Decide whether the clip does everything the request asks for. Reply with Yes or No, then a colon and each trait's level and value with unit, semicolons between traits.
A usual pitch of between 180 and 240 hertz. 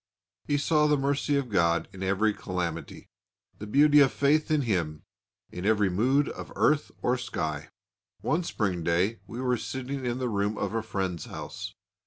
No: low, 115 Hz